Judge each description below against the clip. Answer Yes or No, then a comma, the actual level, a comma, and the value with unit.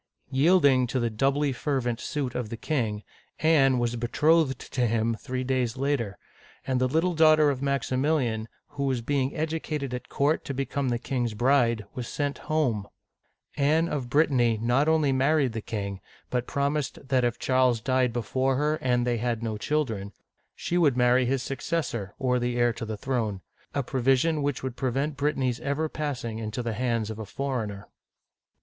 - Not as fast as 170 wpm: No, average, 180 wpm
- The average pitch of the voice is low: Yes, low, 130 Hz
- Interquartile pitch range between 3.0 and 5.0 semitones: Yes, average, 3.3 semitones